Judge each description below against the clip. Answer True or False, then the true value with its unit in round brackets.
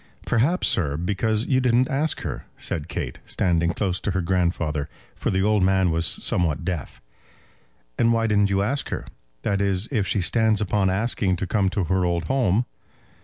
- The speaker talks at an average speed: True (180 wpm)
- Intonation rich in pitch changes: False (3.8 semitones)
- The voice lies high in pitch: False (95 Hz)